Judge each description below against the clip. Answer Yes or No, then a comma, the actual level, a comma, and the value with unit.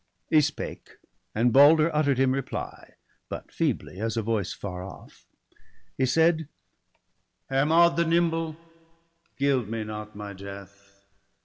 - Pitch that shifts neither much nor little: No, wide, 7.0 semitones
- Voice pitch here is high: No, low, 130 Hz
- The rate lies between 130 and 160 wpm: Yes, slow, 135 wpm